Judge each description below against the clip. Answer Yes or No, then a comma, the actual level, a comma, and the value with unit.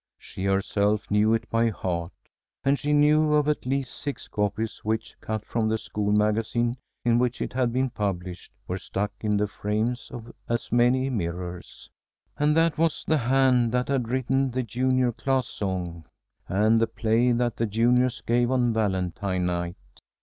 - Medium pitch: No, low, 115 Hz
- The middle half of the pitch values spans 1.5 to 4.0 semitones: Yes, average, 3.7 semitones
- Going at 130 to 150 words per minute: No, average, 170 wpm